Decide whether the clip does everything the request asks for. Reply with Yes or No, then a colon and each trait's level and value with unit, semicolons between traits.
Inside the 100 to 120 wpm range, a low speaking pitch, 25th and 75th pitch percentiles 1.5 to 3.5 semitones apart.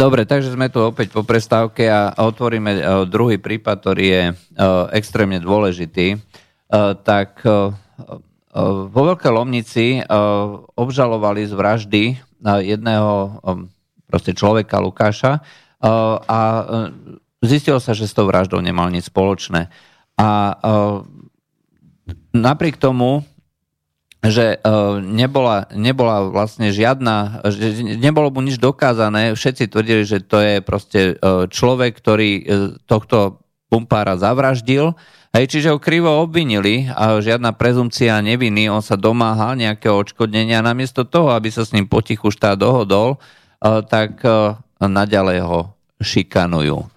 Yes: slow, 110 wpm; low, 110 Hz; average, 2.9 semitones